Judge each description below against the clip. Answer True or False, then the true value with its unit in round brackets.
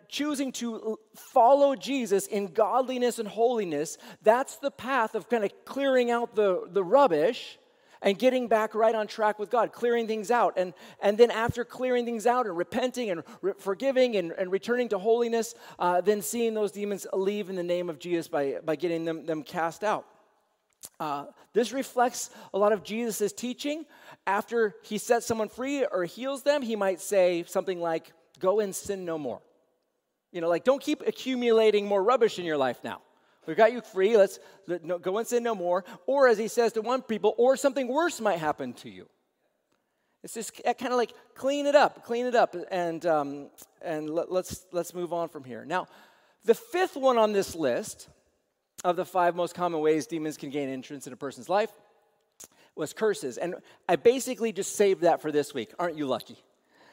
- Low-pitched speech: False (215 Hz)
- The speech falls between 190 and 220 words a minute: True (195 wpm)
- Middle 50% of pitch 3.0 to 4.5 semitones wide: False (5.3 semitones)